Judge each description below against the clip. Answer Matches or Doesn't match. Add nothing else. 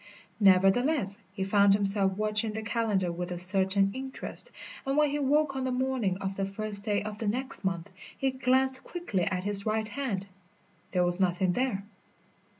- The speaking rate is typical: Matches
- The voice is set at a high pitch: Matches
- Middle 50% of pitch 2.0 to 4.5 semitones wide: Doesn't match